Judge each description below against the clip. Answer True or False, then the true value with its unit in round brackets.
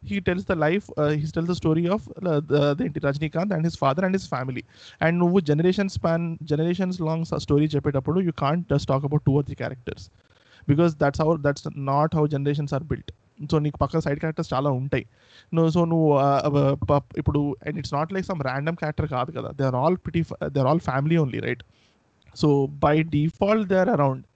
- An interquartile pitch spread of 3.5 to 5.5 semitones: False (3.1 semitones)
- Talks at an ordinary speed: False (185 wpm)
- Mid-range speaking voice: True (150 Hz)